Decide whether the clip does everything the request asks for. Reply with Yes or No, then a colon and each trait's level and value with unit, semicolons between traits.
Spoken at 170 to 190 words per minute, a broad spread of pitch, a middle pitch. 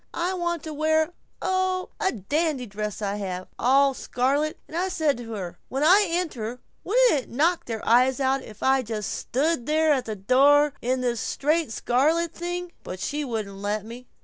No: average, 185 wpm; wide, 6.1 semitones; very high, 275 Hz